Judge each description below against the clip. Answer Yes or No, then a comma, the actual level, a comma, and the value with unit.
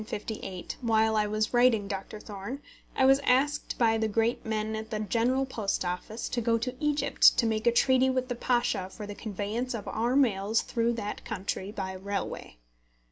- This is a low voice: No, high, 225 Hz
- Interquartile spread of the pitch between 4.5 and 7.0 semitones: No, average, 3.0 semitones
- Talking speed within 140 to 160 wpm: No, average, 200 wpm